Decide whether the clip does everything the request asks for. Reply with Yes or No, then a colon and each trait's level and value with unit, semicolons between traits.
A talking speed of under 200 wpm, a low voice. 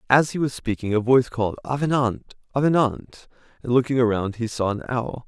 Yes: average, 180 wpm; low, 120 Hz